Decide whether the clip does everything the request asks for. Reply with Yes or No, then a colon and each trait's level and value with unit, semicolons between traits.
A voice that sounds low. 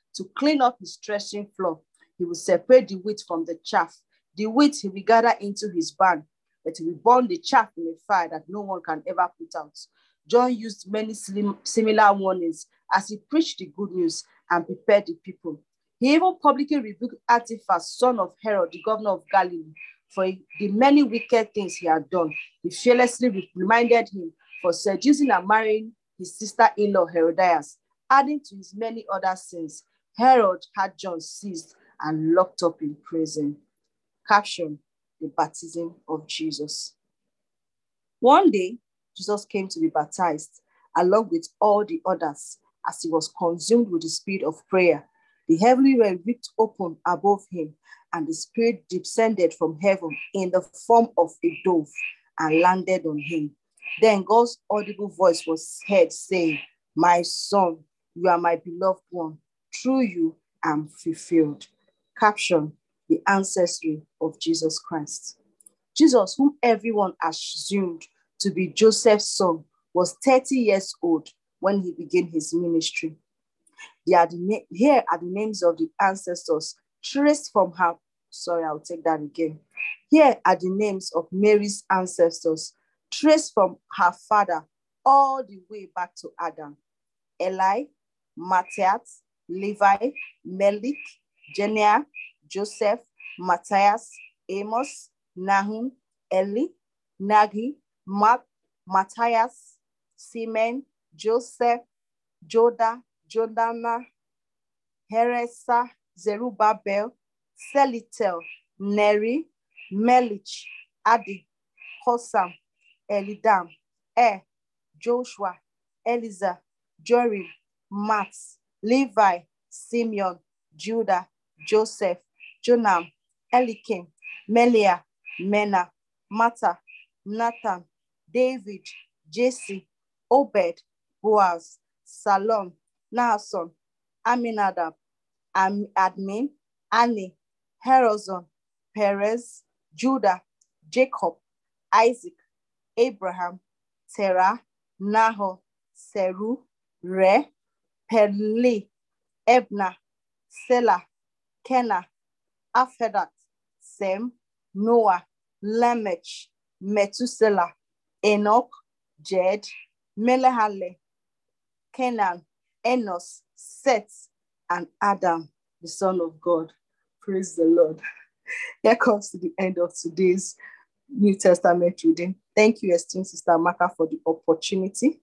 No: high, 195 Hz